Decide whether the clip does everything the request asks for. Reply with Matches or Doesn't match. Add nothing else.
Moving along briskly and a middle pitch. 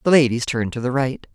Doesn't match